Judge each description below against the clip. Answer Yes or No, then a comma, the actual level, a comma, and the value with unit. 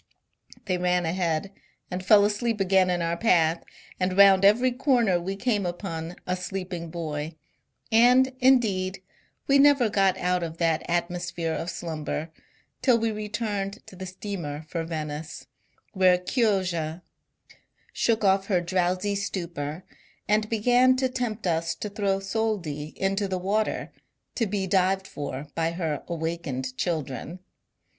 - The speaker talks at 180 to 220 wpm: No, average, 140 wpm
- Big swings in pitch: No, average, 3.8 semitones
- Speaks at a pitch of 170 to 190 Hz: Yes, medium, 185 Hz